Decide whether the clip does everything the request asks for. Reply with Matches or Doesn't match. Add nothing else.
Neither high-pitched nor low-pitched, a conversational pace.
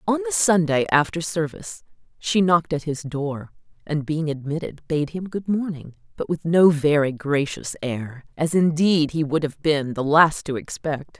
Matches